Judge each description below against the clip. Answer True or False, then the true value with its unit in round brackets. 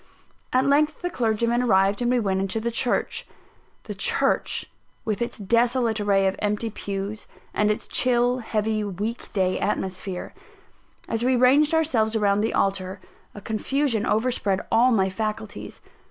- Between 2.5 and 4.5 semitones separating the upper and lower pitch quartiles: True (3.4 semitones)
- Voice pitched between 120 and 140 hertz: False (220 Hz)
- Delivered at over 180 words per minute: False (150 wpm)